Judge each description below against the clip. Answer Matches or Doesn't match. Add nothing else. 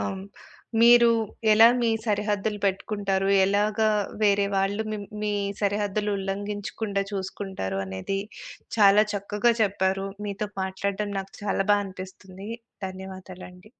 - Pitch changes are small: Matches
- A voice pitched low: Doesn't match